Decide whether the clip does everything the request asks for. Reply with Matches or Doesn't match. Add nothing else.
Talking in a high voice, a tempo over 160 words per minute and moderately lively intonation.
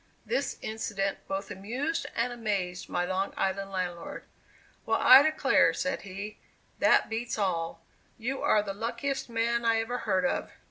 Doesn't match